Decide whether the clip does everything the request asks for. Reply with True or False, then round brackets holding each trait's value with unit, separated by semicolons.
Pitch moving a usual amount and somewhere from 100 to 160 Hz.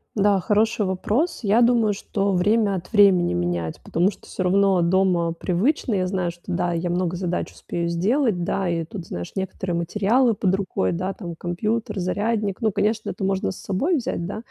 False (3.2 semitones; 190 Hz)